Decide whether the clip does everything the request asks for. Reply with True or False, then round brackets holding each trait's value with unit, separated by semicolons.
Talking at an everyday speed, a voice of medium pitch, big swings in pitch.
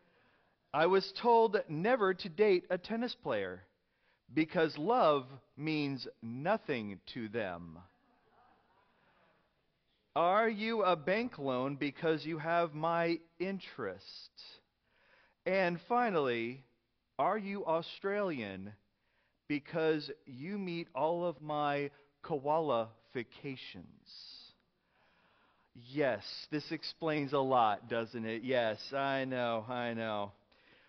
False (95 wpm; 150 Hz; 6.5 semitones)